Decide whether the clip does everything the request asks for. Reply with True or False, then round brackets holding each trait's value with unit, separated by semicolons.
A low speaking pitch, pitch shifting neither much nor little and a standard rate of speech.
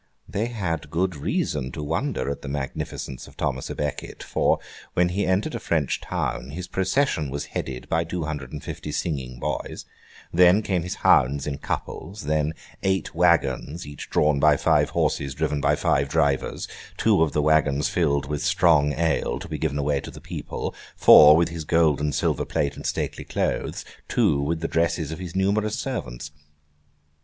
True (75 Hz; 3.4 semitones; 180 wpm)